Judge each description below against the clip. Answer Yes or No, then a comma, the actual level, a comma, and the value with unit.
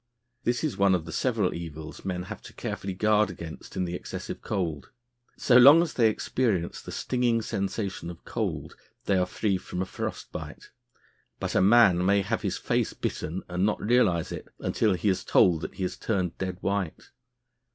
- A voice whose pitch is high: No, very low, 95 Hz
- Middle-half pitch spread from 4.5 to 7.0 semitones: No, average, 3.5 semitones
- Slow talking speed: No, average, 190 wpm